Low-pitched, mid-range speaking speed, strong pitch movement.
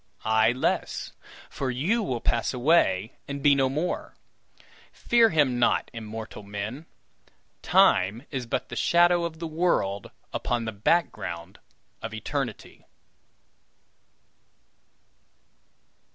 No: low, 125 Hz; slow, 110 wpm; wide, 6.3 semitones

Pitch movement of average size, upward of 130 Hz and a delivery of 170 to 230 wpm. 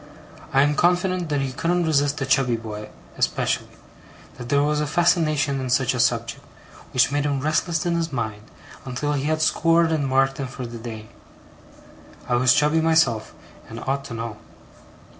Yes: average, 4.1 semitones; medium, 140 Hz; average, 180 wpm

